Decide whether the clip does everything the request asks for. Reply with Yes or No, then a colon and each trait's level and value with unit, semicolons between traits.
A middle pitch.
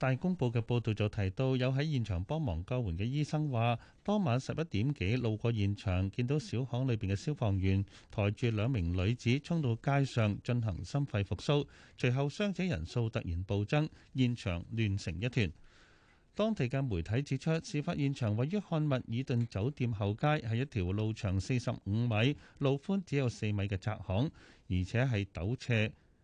No: low, 120 Hz